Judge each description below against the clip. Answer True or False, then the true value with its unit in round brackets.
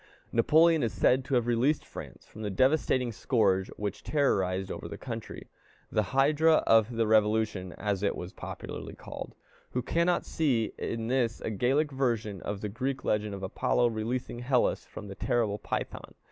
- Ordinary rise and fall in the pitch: True (4.1 semitones)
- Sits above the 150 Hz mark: False (115 Hz)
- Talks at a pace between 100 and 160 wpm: False (170 wpm)